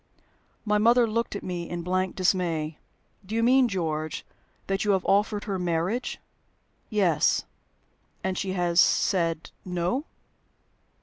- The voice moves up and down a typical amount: Yes, average, 3.5 semitones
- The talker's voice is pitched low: No, medium, 185 Hz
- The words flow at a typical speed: No, slow, 130 wpm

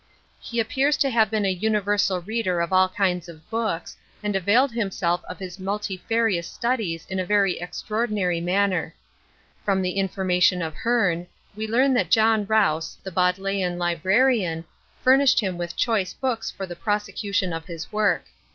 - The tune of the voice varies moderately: Yes, average, 3.5 semitones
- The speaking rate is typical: Yes, average, 160 wpm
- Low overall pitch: No, high, 195 Hz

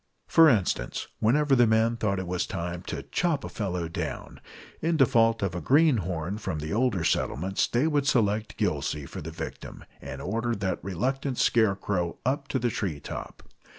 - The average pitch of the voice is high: No, low, 110 Hz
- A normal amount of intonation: No, wide, 6.4 semitones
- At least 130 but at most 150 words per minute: No, average, 175 wpm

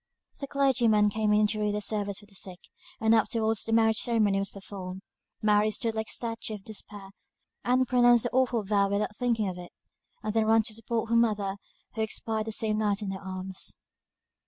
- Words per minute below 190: No, fast, 205 wpm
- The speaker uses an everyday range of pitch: No, narrow, 1.9 semitones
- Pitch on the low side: No, high, 215 Hz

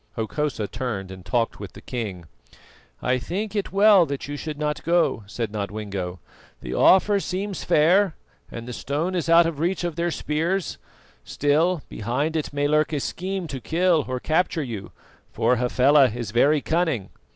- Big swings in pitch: Yes, wide, 6.3 semitones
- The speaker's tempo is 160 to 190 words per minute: Yes, average, 170 wpm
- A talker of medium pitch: Yes, medium, 150 Hz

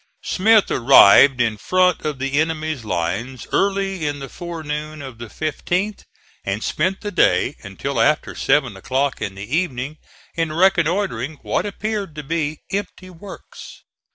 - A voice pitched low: No, medium, 155 Hz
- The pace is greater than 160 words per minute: No, average, 145 wpm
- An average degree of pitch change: No, wide, 5.8 semitones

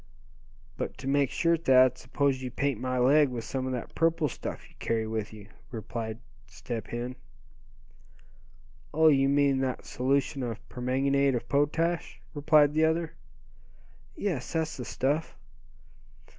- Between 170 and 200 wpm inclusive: No, average, 145 wpm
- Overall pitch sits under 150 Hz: Yes, low, 135 Hz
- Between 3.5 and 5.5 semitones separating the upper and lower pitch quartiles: No, average, 3.1 semitones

